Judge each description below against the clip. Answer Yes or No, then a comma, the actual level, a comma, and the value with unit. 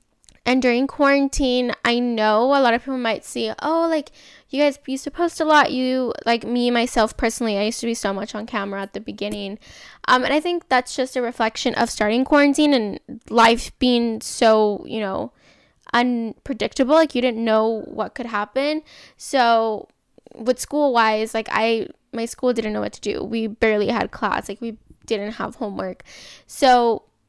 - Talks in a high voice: Yes, high, 240 Hz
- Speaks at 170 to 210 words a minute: Yes, average, 185 wpm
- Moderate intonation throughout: Yes, average, 3.3 semitones